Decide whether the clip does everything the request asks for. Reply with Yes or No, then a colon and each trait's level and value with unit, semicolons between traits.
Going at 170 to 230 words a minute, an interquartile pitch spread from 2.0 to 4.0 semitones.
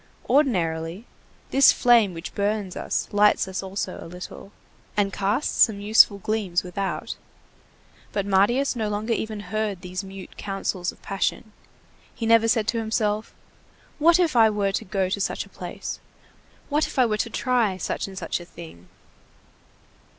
No: average, 160 wpm; average, 2.9 semitones